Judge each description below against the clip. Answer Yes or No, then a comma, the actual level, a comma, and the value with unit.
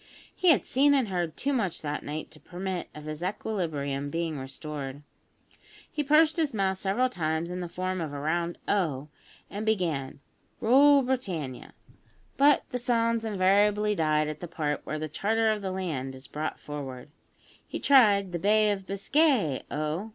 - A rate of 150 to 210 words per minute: Yes, average, 170 wpm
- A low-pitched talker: No, medium, 185 Hz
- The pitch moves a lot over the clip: Yes, wide, 6.3 semitones